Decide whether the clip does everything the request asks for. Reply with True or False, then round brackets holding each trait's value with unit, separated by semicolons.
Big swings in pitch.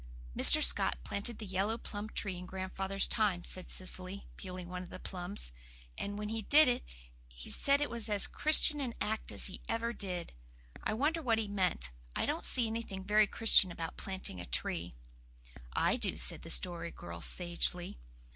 False (3.7 semitones)